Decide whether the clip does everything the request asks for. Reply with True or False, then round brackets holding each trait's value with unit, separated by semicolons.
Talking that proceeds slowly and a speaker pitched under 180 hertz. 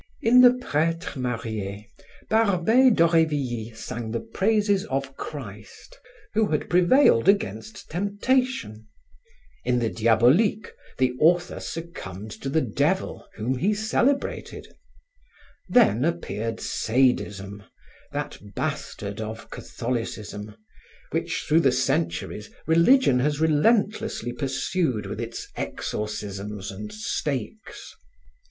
True (100 wpm; 135 Hz)